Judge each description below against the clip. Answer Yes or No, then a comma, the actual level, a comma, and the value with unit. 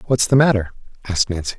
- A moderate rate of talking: Yes, average, 190 wpm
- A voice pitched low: Yes, low, 110 Hz